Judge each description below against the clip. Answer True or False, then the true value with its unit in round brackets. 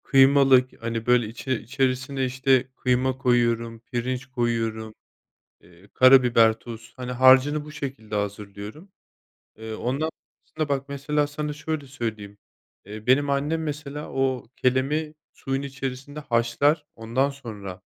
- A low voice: True (130 Hz)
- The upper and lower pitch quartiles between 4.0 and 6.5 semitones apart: False (3.3 semitones)